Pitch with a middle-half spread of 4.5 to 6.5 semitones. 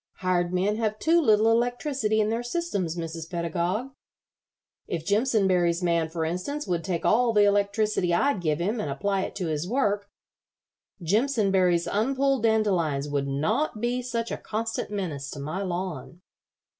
Yes: average, 4.9 semitones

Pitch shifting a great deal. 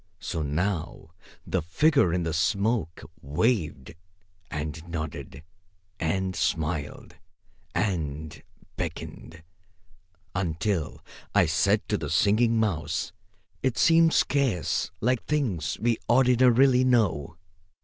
Yes: wide, 7.1 semitones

